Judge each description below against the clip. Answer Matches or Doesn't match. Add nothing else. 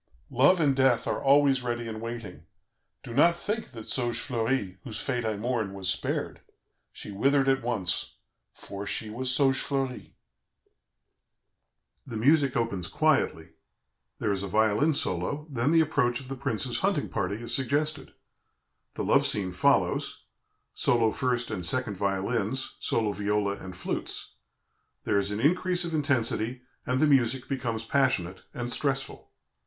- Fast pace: Doesn't match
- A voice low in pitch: Matches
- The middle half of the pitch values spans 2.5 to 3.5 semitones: Doesn't match